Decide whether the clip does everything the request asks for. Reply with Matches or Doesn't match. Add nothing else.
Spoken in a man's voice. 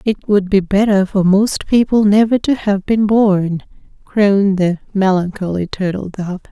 Doesn't match